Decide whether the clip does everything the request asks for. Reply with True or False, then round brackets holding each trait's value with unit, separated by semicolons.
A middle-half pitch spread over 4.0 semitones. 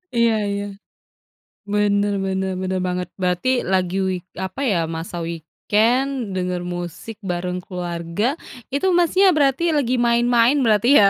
True (4.6 semitones)